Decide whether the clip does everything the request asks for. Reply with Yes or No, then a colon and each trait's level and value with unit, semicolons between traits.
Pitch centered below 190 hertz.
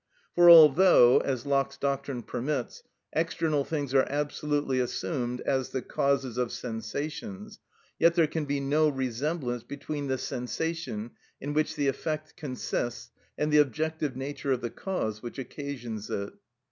Yes: medium, 140 Hz